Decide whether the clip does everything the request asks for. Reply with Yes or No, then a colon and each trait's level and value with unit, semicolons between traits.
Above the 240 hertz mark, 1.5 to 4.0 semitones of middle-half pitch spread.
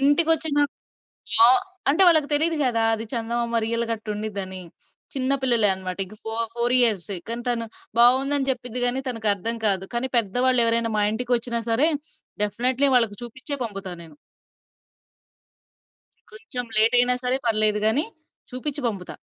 No: high, 235 Hz; average, 3.0 semitones